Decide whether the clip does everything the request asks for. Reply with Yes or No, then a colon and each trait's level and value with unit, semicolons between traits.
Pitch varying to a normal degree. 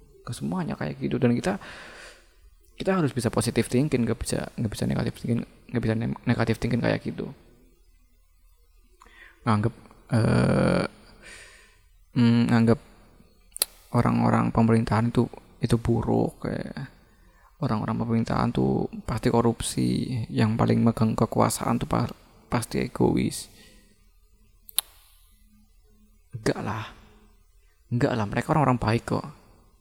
No: wide, 6.2 semitones